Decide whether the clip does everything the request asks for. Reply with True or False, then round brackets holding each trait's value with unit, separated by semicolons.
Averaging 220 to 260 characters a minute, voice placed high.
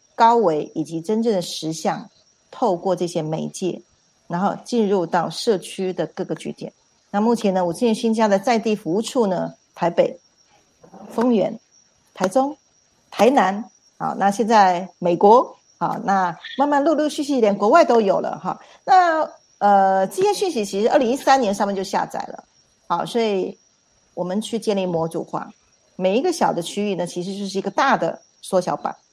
True (250 characters per minute; 205 Hz)